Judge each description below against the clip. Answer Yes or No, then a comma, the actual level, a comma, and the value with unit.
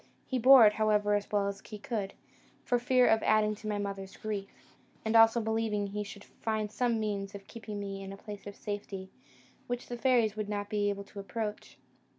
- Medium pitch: No, high, 210 Hz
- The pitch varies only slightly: Yes, narrow, 1.7 semitones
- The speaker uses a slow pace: No, fast, 205 wpm